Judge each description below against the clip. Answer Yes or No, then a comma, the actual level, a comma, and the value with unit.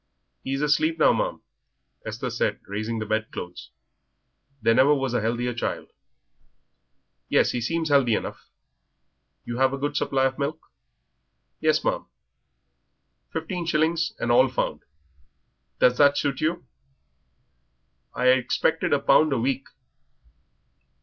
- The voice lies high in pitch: No, low, 130 Hz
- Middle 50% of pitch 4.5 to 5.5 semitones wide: No, average, 3.7 semitones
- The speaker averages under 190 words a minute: Yes, slow, 135 wpm